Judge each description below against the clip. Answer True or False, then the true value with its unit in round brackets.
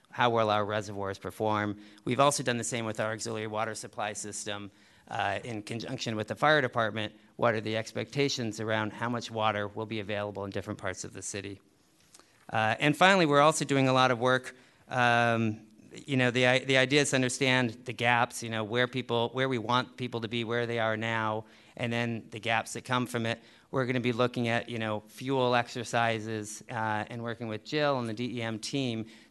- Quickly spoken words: True (210 wpm)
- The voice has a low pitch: True (115 Hz)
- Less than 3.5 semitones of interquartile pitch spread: True (2.5 semitones)